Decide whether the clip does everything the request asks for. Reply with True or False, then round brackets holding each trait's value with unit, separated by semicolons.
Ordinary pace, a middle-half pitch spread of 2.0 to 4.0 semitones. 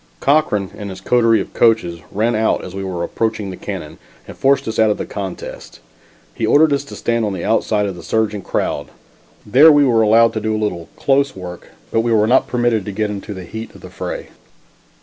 False (225 wpm; 3.0 semitones)